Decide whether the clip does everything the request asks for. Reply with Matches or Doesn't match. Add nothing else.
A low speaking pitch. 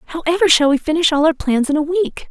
Doesn't match